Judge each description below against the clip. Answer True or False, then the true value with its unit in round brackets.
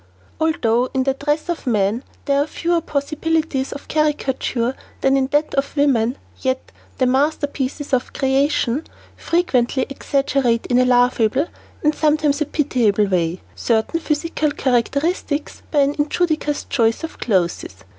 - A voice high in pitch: True (275 Hz)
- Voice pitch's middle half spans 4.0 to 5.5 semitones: False (3.5 semitones)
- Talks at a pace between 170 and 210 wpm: False (135 wpm)